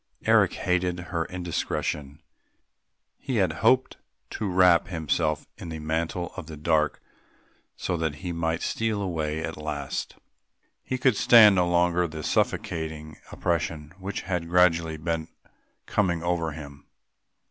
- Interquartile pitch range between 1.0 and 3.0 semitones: Yes, narrow, 2.4 semitones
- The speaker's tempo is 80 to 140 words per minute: Yes, slow, 135 wpm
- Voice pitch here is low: Yes, very low, 85 Hz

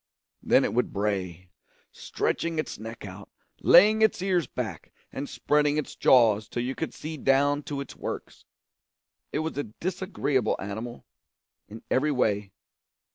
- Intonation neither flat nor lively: No, wide, 6.3 semitones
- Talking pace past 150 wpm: No, average, 145 wpm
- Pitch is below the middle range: Yes, low, 130 Hz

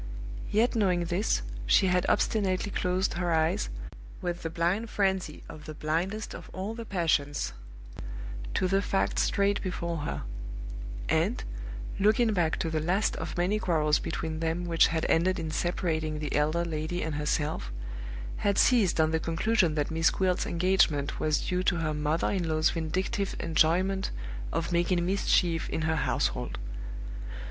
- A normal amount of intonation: Yes, average, 3.2 semitones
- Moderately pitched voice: Yes, medium, 170 Hz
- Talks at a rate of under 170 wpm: Yes, average, 155 wpm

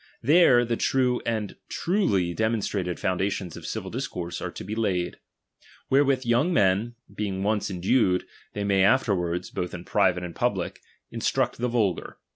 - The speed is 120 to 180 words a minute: Yes, average, 155 wpm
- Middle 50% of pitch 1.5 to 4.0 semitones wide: No, average, 4.8 semitones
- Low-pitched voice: Yes, low, 100 Hz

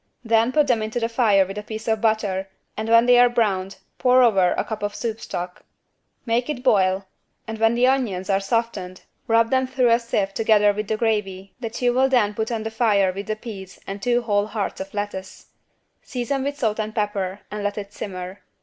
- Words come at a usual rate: No, fast, 215 wpm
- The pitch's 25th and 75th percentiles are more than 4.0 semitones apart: No, average, 3.0 semitones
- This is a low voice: No, high, 220 Hz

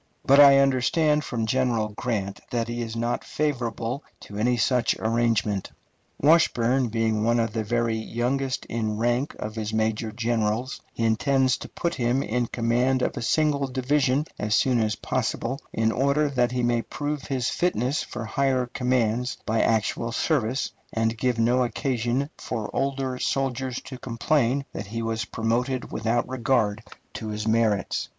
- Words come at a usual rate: Yes, average, 160 wpm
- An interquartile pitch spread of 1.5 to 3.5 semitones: Yes, average, 2.8 semitones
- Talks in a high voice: No, low, 120 Hz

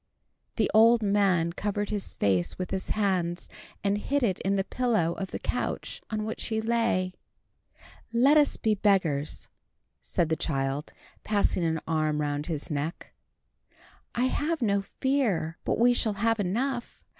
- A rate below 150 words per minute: No, average, 155 wpm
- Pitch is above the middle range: Yes, high, 200 Hz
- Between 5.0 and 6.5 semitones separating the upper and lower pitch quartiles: Yes, wide, 5.5 semitones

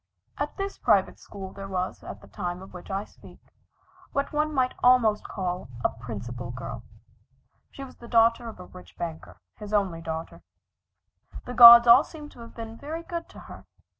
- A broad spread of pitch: Yes, wide, 5.7 semitones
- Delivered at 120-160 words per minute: No, average, 185 wpm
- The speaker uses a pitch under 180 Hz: No, high, 215 Hz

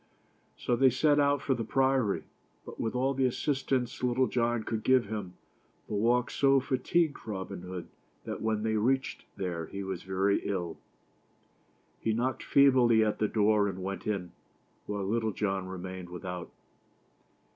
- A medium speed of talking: Yes, average, 155 wpm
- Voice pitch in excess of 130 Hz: No, low, 110 Hz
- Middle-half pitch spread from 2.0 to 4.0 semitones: No, average, 5.1 semitones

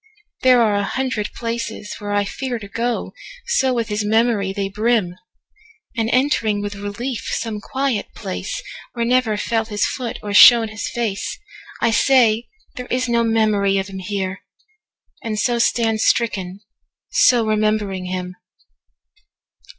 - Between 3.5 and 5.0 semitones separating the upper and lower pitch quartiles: No, average, 2.9 semitones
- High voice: Yes, high, 220 Hz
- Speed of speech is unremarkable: No, slow, 125 wpm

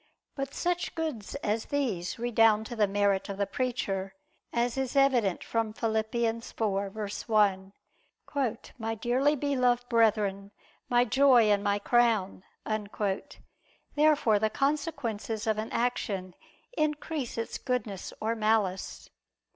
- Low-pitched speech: No, high, 225 Hz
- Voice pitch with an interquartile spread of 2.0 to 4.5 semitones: Yes, average, 3.5 semitones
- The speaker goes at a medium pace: No, slow, 115 wpm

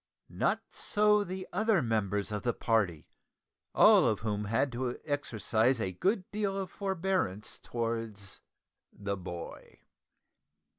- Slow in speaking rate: Yes, slow, 120 wpm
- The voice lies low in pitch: Yes, low, 115 Hz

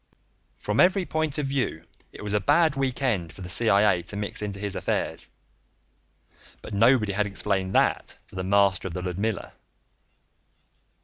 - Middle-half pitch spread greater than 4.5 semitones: Yes, average, 5.2 semitones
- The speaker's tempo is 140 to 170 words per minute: Yes, average, 165 wpm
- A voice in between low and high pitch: No, low, 105 Hz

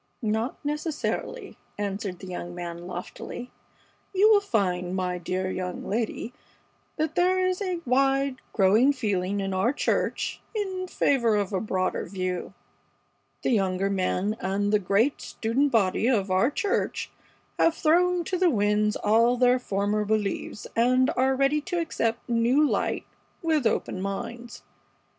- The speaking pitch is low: No, high, 225 Hz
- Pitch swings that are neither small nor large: No, wide, 6.4 semitones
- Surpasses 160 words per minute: No, average, 145 wpm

